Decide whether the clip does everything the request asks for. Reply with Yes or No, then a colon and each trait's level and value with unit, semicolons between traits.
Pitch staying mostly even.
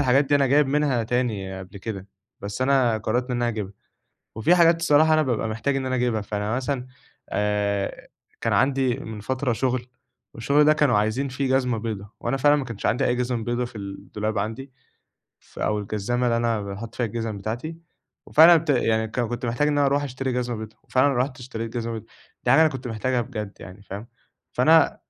No: average, 3.7 semitones